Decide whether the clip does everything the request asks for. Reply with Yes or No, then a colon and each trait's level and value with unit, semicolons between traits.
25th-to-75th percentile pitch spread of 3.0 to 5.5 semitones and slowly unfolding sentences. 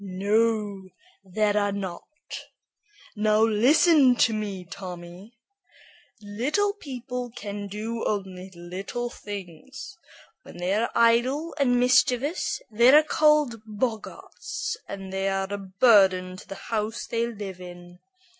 Yes: average, 4.2 semitones; slow, 120 wpm